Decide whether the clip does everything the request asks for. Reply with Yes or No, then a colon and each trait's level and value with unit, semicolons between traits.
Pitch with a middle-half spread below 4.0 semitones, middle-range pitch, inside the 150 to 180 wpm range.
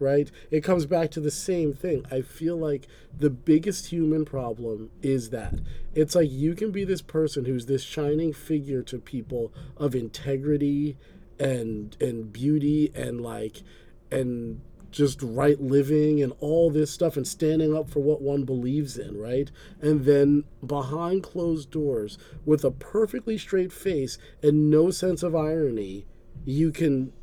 Yes: average, 3.1 semitones; medium, 145 Hz; average, 155 wpm